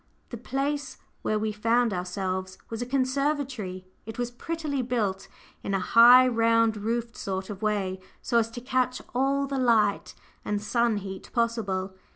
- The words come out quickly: No, average, 160 wpm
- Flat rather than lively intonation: No, average, 3.9 semitones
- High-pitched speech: Yes, high, 230 Hz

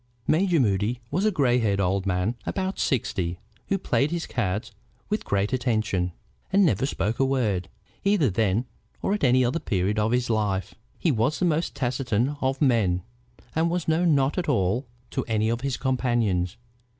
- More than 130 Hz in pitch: No, low, 120 Hz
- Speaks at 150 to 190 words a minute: Yes, average, 180 wpm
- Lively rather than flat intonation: Yes, wide, 6.1 semitones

